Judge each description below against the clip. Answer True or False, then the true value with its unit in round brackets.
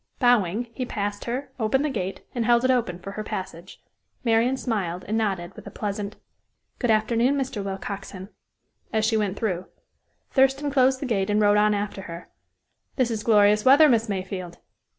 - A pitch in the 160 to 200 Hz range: False (215 Hz)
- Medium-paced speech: True (175 wpm)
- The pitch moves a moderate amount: True (3.7 semitones)